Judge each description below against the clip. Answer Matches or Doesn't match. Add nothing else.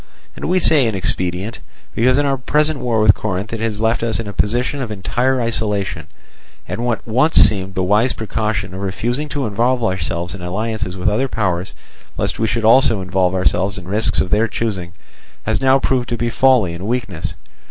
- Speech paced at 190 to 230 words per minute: Matches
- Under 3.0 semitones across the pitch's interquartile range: Doesn't match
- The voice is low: Matches